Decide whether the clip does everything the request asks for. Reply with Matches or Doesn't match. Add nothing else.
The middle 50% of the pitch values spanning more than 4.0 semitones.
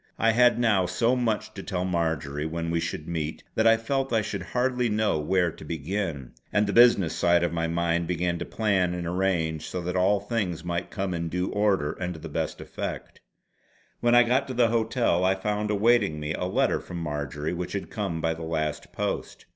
Matches